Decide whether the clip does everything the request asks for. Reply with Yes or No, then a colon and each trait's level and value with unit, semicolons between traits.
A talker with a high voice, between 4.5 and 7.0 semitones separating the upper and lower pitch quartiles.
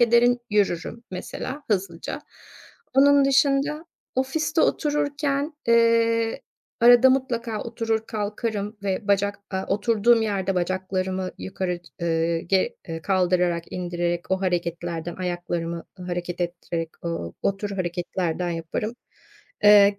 Yes: high, 195 Hz; average, 5.0 semitones